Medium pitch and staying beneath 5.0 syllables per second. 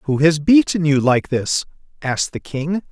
Yes: medium, 155 Hz; 4.5 syllables/s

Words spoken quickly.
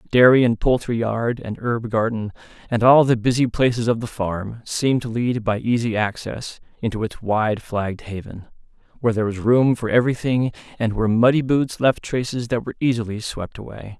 No: average, 185 wpm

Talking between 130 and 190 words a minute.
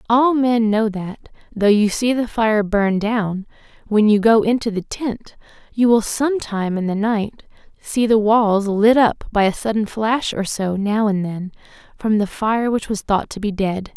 No: average, 200 wpm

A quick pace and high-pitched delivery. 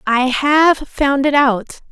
No: average, 155 wpm; very high, 275 Hz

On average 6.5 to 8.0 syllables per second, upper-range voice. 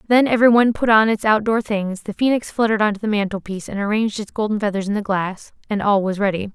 Yes: 6.8 syllables/s; high, 210 Hz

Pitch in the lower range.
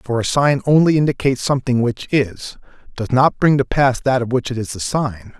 Yes: low, 130 Hz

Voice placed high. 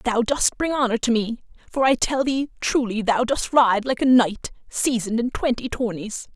Yes: high, 240 Hz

